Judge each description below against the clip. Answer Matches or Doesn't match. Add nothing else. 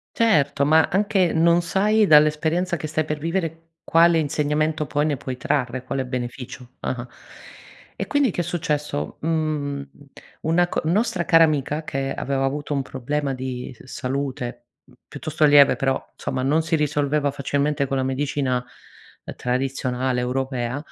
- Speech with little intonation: Doesn't match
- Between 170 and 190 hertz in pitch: Doesn't match